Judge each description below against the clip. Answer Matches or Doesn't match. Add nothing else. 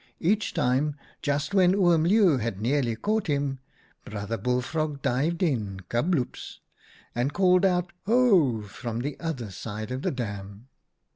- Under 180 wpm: Matches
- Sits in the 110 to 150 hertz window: Matches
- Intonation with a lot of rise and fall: Matches